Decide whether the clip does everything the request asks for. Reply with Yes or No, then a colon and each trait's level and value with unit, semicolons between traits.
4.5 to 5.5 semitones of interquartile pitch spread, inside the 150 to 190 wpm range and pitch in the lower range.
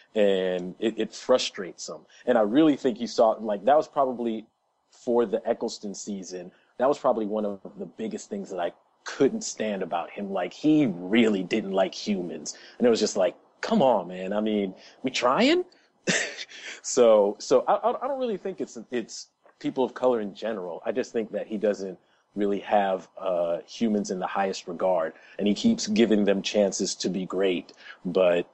Yes: average, 5.2 semitones; average, 185 wpm; low, 110 Hz